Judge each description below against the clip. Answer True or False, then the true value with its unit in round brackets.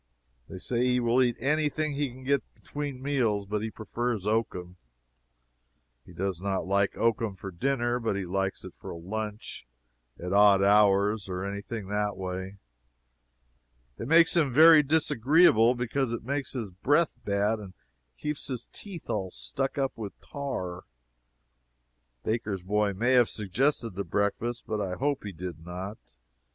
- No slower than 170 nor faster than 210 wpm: False (160 wpm)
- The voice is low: True (110 Hz)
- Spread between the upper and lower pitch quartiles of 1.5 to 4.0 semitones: False (5.1 semitones)